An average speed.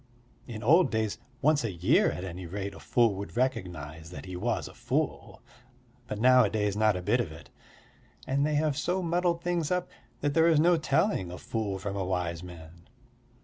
Yes: average, 190 wpm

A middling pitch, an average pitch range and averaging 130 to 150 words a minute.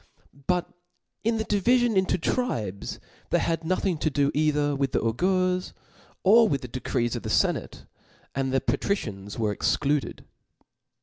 No: medium, 150 Hz; wide, 6.6 semitones; average, 145 wpm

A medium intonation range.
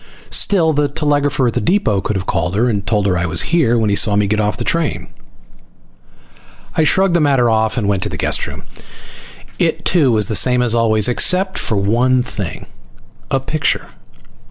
No: wide, 5.8 semitones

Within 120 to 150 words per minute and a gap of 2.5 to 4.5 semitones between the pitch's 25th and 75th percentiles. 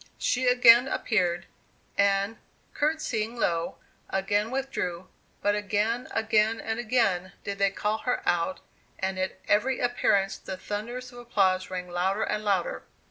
Yes: slow, 135 wpm; average, 4.1 semitones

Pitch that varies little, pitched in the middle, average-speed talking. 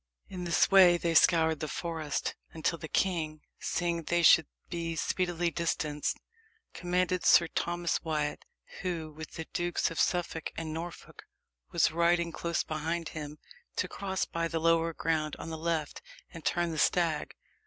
Yes: narrow, 1.5 semitones; medium, 165 Hz; average, 155 wpm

